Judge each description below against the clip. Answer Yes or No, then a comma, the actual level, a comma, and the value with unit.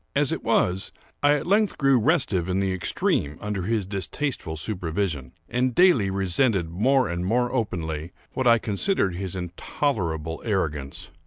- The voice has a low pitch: Yes, very low, 95 Hz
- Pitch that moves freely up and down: Yes, wide, 6.4 semitones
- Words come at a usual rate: Yes, average, 150 wpm